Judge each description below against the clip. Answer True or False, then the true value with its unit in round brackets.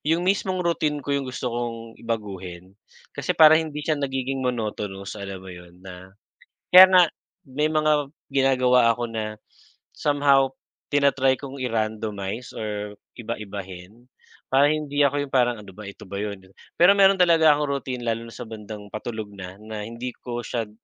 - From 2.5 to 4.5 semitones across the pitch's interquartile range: False (5.4 semitones)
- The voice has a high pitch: False (120 Hz)